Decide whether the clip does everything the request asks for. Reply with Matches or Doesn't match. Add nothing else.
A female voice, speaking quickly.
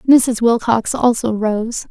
Doesn't match